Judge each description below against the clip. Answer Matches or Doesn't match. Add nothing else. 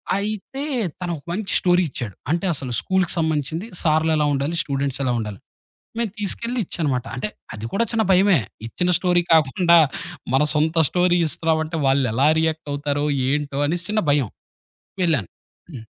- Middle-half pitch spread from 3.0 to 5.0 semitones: Matches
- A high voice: Doesn't match